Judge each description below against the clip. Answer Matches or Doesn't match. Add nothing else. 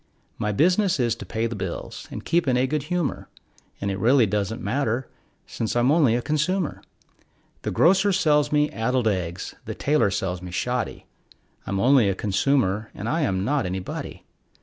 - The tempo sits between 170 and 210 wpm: Matches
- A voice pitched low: Matches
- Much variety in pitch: Matches